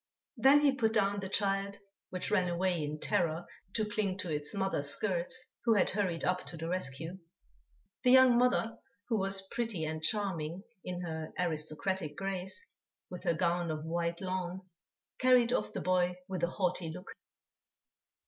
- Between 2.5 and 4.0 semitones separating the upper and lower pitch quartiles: Yes, average, 3.2 semitones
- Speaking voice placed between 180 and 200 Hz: Yes, medium, 185 Hz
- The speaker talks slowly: No, average, 165 wpm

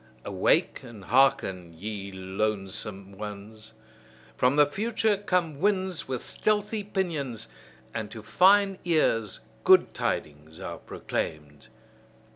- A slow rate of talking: Yes, slow, 105 wpm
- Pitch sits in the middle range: No, low, 115 Hz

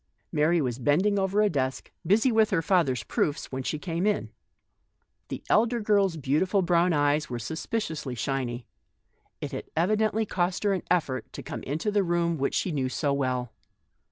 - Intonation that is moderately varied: No, wide, 6.2 semitones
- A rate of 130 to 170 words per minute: No, average, 180 wpm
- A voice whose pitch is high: No, medium, 165 Hz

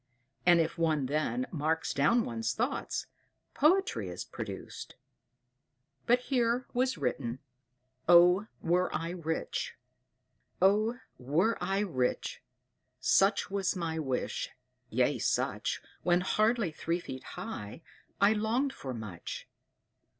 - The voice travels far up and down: Yes, wide, 6.3 semitones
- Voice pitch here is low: No, medium, 175 Hz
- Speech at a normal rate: No, slow, 115 wpm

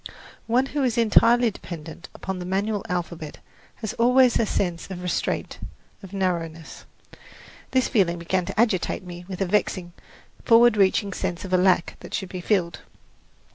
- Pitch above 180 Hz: Yes, high, 190 Hz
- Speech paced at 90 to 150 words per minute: No, average, 160 wpm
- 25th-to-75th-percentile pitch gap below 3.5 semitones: No, average, 4.1 semitones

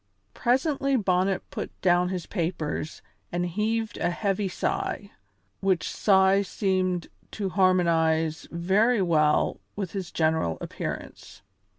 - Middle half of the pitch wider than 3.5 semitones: No, average, 3.1 semitones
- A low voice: No, medium, 185 Hz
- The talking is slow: Yes, slow, 110 wpm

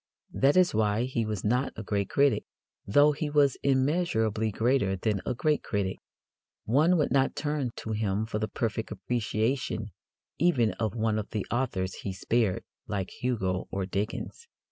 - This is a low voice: Yes, low, 110 Hz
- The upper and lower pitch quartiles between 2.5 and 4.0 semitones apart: No, average, 4.6 semitones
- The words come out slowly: No, average, 165 wpm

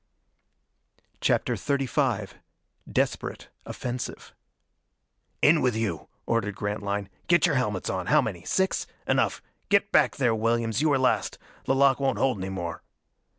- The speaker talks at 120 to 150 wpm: Yes, slow, 135 wpm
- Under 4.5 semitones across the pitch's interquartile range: No, average, 5.2 semitones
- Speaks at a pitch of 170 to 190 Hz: No, low, 120 Hz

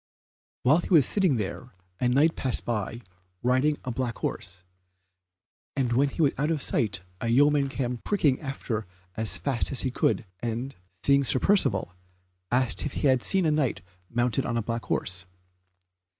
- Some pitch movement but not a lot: Yes, average, 3.5 semitones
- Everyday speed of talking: Yes, average, 170 wpm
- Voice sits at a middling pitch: No, low, 130 Hz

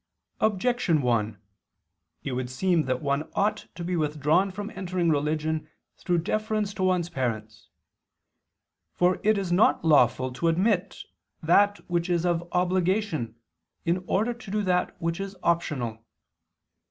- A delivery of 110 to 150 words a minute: Yes, average, 140 wpm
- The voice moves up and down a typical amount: Yes, average, 4.4 semitones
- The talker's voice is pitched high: No, medium, 175 Hz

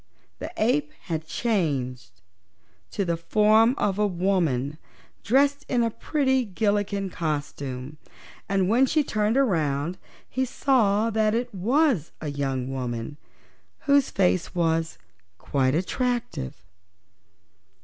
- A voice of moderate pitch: No, high, 195 Hz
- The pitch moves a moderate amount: No, wide, 7.9 semitones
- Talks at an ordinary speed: No, slow, 115 wpm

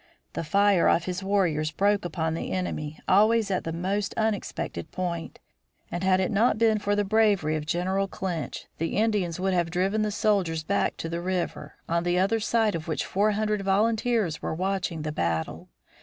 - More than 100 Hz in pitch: Yes, high, 190 Hz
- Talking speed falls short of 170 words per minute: No, average, 185 wpm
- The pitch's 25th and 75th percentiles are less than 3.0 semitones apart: No, average, 3.6 semitones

